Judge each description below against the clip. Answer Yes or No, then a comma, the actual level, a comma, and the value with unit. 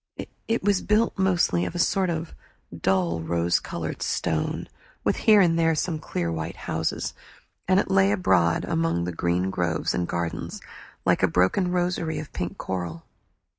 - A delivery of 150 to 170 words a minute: Yes, average, 165 wpm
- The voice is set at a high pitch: No, very low, 95 Hz